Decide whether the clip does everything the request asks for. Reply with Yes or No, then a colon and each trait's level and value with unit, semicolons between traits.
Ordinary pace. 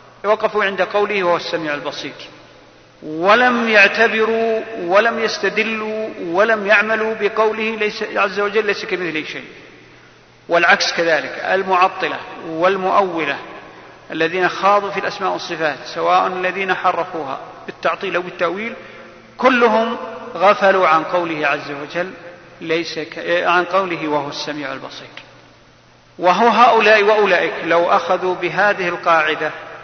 Yes: average, 110 wpm